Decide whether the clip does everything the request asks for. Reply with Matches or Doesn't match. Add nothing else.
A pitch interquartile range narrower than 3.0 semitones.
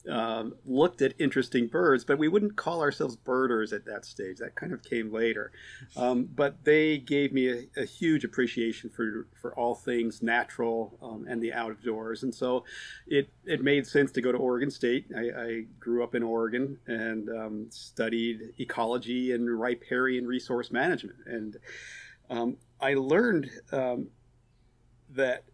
Matches